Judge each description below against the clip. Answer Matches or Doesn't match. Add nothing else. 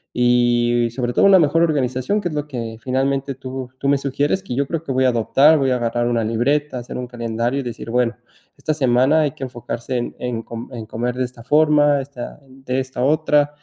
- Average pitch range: Matches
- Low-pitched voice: Matches